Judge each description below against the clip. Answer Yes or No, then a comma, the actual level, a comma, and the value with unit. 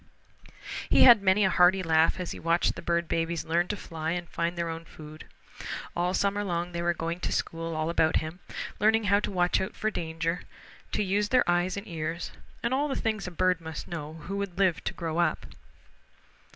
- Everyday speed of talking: No, fast, 215 wpm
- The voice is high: No, medium, 175 Hz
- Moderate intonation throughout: Yes, average, 3.0 semitones